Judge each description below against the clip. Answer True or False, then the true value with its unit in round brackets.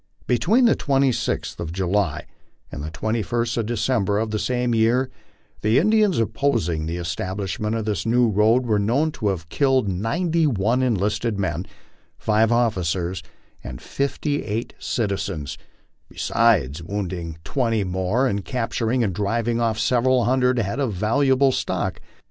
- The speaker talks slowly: False (145 wpm)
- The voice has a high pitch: False (110 Hz)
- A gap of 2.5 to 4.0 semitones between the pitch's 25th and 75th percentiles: False (4.6 semitones)